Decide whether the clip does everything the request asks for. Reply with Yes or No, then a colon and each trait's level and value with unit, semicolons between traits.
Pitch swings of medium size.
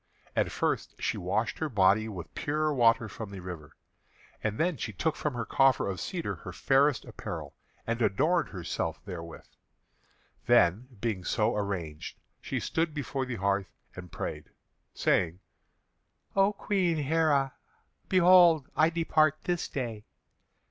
No: wide, 7.9 semitones